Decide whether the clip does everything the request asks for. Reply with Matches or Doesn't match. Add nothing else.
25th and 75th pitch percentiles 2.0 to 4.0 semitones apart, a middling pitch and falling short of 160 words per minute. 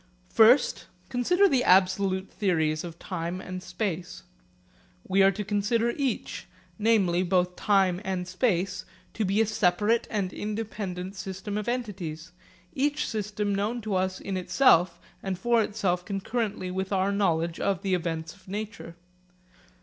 Doesn't match